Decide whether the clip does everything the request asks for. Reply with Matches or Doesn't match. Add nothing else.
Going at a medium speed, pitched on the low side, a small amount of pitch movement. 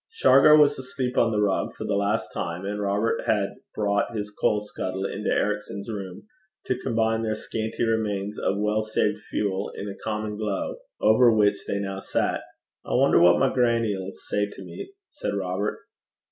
Matches